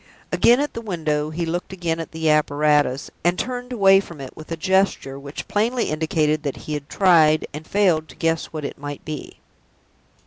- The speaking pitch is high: No, medium, 160 Hz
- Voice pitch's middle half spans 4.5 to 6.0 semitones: No, average, 4.0 semitones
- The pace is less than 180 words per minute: No, average, 195 wpm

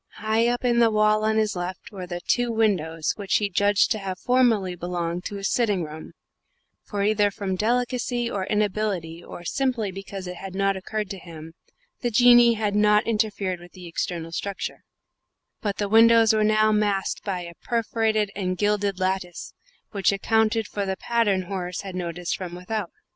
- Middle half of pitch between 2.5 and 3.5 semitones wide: Yes, average, 3.1 semitones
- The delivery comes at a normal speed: Yes, average, 180 wpm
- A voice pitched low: No, high, 205 Hz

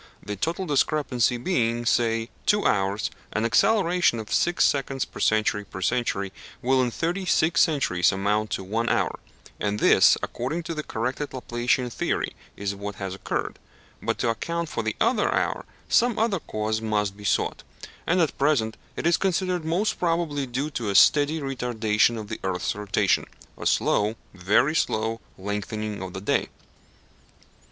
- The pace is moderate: Yes, average, 160 wpm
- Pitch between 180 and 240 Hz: No, low, 120 Hz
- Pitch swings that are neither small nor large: No, wide, 6.7 semitones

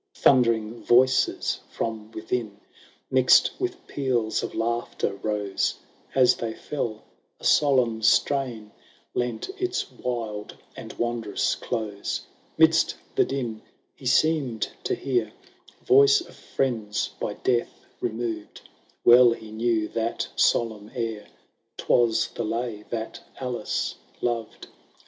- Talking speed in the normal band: No, slow, 115 wpm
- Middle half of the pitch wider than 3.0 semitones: No, narrow, 2.5 semitones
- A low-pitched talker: Yes, low, 115 Hz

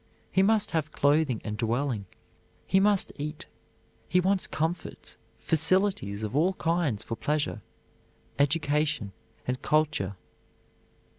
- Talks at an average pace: No, slow, 115 wpm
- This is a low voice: No, medium, 150 Hz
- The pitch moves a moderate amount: No, wide, 5.7 semitones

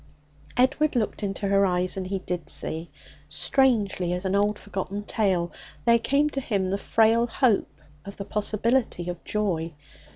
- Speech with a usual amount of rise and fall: Yes, average, 3.8 semitones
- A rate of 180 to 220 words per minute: No, average, 160 wpm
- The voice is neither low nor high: No, high, 200 Hz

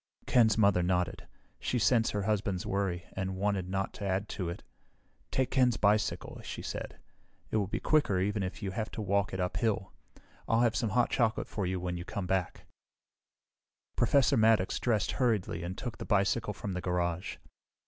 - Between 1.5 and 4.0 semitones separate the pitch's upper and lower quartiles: Yes, average, 3.1 semitones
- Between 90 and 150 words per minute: No, average, 180 wpm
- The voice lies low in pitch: Yes, low, 100 Hz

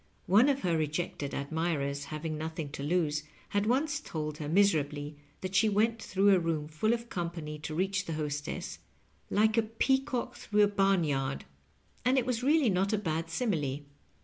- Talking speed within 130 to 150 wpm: No, average, 175 wpm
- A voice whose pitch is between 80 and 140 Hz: No, medium, 175 Hz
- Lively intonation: Yes, wide, 6.0 semitones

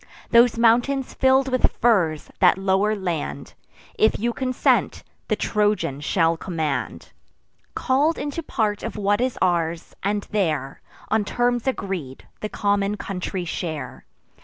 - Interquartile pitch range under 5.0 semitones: No, wide, 5.6 semitones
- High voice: Yes, high, 205 Hz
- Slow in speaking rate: Yes, slow, 130 wpm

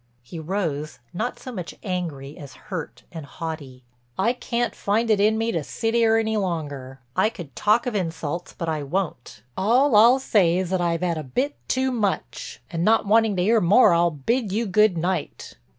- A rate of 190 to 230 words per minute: Yes, average, 195 wpm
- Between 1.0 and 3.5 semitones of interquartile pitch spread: No, wide, 5.5 semitones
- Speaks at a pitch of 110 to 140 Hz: No, medium, 185 Hz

